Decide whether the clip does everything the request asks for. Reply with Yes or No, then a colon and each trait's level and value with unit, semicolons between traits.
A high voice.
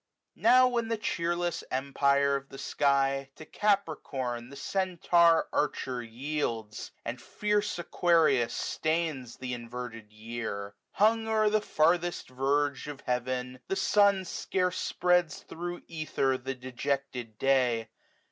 No: medium, 140 Hz